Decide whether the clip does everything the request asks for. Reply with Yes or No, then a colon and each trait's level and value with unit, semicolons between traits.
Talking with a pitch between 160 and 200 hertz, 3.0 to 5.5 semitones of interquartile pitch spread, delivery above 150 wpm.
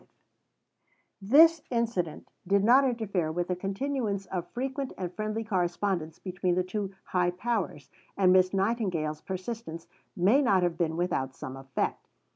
No: high, 190 Hz; average, 4.4 semitones; average, 145 wpm